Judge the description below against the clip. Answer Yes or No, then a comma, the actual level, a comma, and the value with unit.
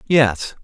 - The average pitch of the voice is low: Yes, low, 125 Hz